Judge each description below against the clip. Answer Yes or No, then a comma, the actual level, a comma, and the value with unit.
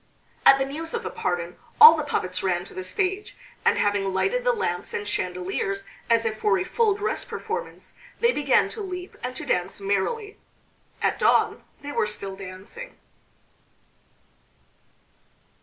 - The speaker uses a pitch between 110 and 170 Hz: No, high, 215 Hz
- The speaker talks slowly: No, average, 155 wpm